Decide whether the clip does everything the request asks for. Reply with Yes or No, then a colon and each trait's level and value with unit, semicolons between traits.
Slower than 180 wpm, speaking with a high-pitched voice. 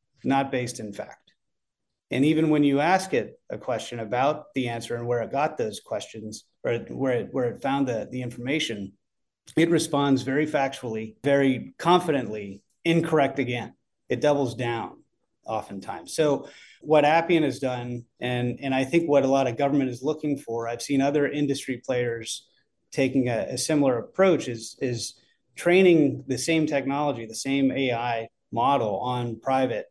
No: average, 165 wpm; low, 135 Hz